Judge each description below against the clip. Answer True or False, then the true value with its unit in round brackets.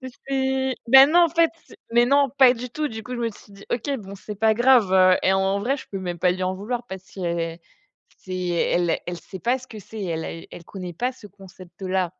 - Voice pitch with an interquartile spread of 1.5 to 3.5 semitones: False (5.4 semitones)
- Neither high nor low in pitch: False (205 Hz)